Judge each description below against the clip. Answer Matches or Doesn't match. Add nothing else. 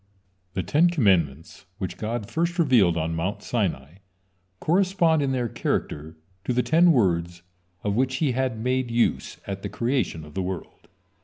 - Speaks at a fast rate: Doesn't match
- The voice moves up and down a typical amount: Doesn't match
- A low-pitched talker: Matches